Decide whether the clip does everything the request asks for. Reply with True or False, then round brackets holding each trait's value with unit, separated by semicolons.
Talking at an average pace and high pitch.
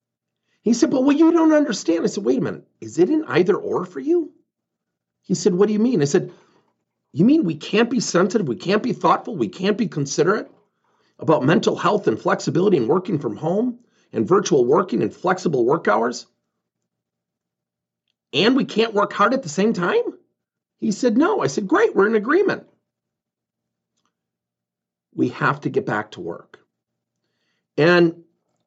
True (175 wpm; 205 Hz)